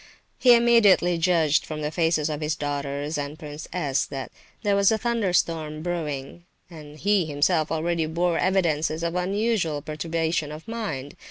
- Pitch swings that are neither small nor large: Yes, average, 3.2 semitones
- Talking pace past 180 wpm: No, average, 155 wpm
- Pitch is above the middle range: No, medium, 160 Hz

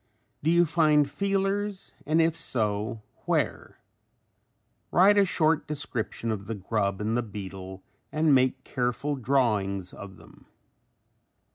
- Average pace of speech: No, slow, 125 wpm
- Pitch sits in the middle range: No, low, 130 Hz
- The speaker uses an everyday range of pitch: No, wide, 7.4 semitones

